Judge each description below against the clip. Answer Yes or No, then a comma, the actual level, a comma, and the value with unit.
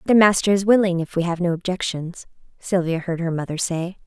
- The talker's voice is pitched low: No, medium, 180 Hz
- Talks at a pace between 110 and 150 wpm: No, fast, 205 wpm